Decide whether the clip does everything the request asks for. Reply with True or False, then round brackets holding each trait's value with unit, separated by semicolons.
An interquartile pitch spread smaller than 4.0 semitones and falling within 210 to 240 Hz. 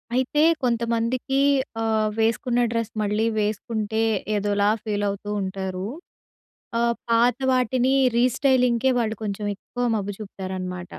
True (2.9 semitones; 220 Hz)